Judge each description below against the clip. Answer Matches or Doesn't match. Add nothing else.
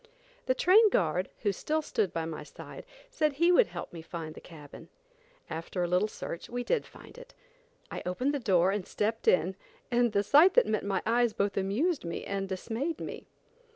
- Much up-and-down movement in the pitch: Matches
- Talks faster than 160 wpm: Matches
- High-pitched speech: Matches